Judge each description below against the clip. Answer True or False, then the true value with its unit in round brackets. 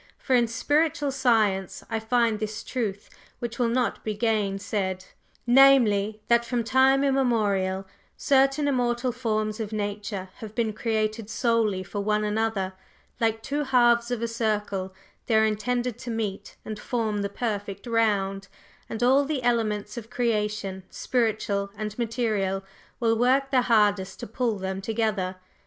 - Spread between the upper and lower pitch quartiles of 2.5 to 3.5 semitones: True (2.8 semitones)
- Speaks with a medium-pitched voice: False (220 Hz)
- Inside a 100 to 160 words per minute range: True (145 wpm)